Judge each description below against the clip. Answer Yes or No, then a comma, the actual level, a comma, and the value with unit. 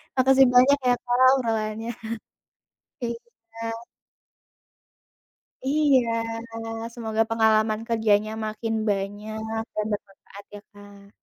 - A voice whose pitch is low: No, high, 225 Hz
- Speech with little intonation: Yes, narrow, 2.3 semitones